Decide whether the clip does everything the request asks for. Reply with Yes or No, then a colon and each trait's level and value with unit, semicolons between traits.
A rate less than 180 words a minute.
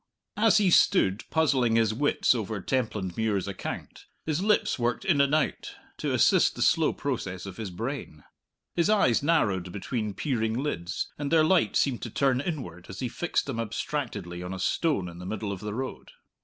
No: average, 185 wpm